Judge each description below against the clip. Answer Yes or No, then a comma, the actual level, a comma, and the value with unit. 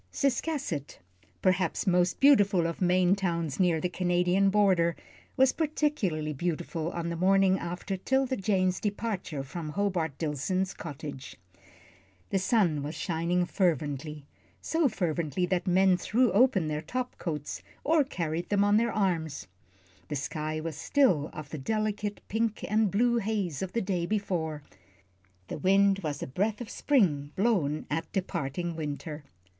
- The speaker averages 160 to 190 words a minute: No, average, 145 wpm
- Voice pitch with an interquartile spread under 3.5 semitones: No, average, 4.4 semitones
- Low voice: No, medium, 180 Hz